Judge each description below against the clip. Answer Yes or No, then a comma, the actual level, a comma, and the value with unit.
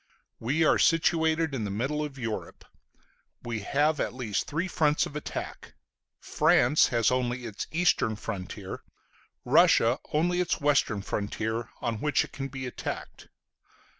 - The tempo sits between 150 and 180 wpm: No, average, 140 wpm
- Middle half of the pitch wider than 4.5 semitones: Yes, average, 5.0 semitones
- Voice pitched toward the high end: No, low, 135 Hz